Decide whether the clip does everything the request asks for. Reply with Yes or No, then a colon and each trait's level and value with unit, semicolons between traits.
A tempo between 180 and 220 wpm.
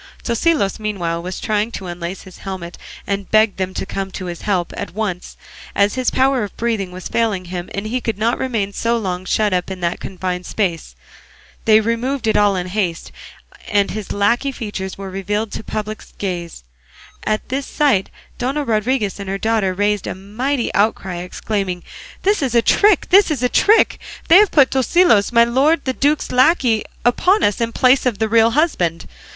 Yes: average, 190 wpm